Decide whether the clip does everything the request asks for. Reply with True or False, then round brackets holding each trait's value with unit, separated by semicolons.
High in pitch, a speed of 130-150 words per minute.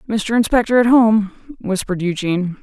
True (210 Hz; 135 wpm)